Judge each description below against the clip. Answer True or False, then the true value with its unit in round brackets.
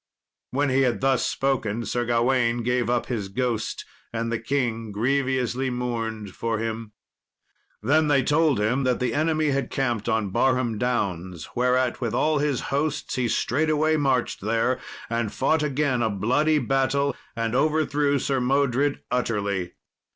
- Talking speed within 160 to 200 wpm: False (150 wpm)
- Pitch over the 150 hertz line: False (125 Hz)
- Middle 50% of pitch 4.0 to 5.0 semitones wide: False (3.3 semitones)